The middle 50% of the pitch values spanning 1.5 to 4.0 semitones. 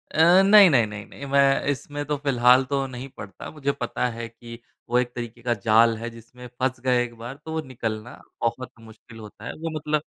Yes: average, 3.2 semitones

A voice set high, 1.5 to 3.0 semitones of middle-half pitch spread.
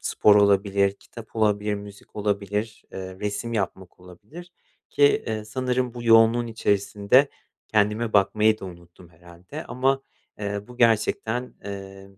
No: low, 105 Hz; average, 2.7 semitones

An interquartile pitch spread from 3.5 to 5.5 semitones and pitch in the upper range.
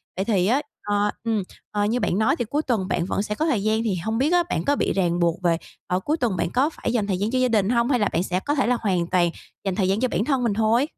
Yes: average, 4.7 semitones; high, 215 Hz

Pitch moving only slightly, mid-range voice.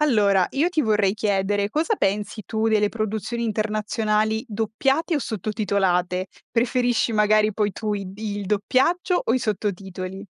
No: narrow, 2.3 semitones; high, 215 Hz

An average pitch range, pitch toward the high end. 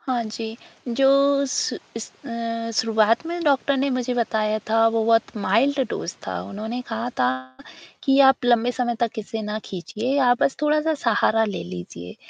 Yes: average, 3.5 semitones; high, 230 Hz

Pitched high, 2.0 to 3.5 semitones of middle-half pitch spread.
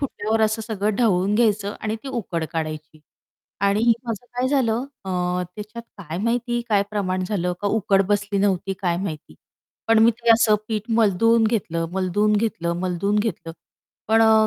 Yes: high, 210 Hz; average, 3.2 semitones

